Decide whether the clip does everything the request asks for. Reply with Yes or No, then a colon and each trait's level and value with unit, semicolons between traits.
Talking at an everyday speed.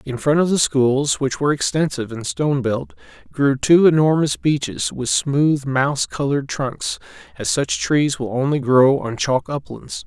Yes: average, 175 wpm